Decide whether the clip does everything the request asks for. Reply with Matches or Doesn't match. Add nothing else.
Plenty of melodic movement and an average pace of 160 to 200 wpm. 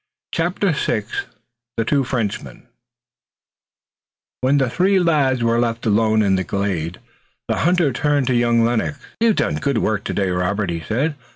Doesn't match